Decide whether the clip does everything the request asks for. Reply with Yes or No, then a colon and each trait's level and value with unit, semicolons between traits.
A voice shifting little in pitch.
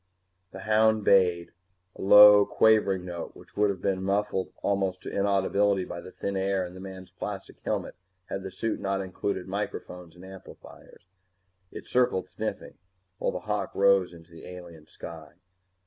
Yes: narrow, 1.9 semitones